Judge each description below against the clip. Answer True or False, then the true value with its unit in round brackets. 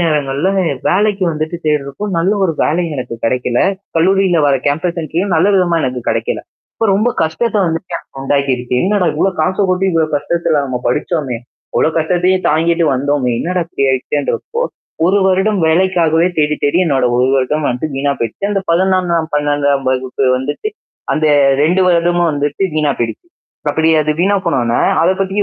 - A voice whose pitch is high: False (160 Hz)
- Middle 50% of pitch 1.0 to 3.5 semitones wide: False (4.4 semitones)